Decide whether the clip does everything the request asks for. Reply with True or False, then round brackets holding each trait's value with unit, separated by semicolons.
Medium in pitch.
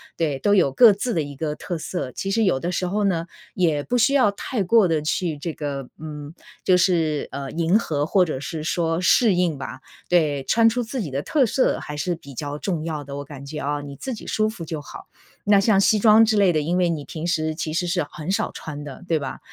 True (165 Hz)